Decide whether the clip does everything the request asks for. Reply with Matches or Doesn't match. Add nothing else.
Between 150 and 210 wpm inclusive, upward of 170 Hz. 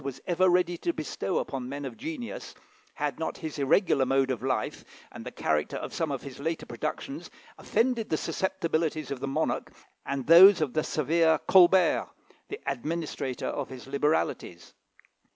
Doesn't match